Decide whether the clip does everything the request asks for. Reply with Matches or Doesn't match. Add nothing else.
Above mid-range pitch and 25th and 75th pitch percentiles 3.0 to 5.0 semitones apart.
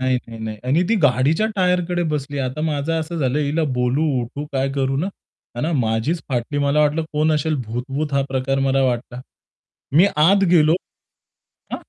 Doesn't match